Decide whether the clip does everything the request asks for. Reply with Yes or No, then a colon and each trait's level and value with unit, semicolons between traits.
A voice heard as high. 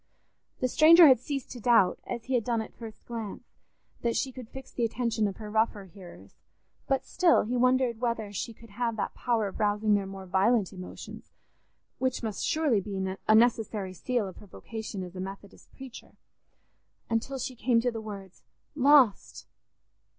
Yes: high, 225 Hz